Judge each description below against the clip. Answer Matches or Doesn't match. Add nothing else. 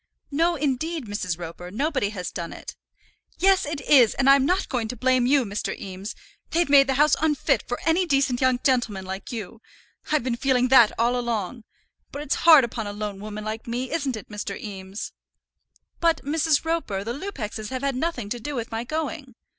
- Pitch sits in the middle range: Doesn't match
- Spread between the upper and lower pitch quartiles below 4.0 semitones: Doesn't match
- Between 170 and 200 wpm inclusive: Matches